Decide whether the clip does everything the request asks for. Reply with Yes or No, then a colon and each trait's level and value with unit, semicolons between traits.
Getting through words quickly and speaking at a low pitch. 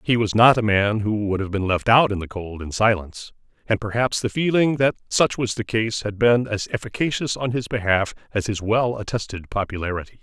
Yes: fast, 215 wpm; low, 110 Hz